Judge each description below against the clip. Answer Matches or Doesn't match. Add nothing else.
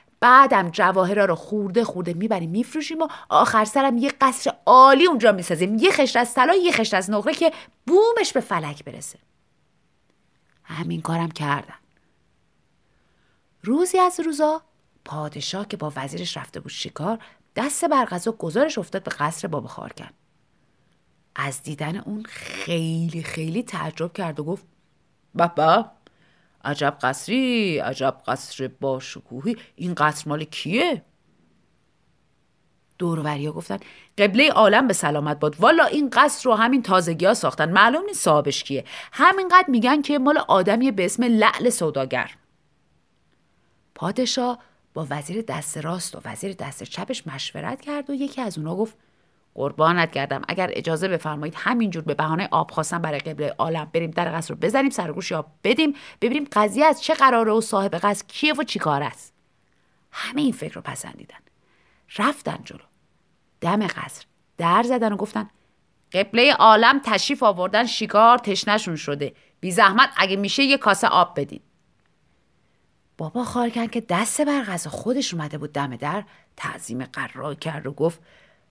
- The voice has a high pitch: Matches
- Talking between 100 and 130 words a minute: Doesn't match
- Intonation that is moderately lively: Doesn't match